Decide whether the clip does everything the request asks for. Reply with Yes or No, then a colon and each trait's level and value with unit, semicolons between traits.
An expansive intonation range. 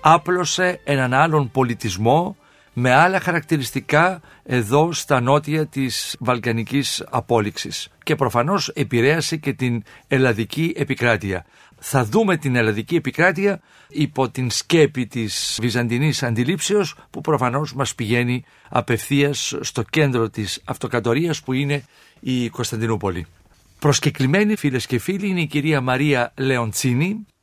No: average, 4.4 semitones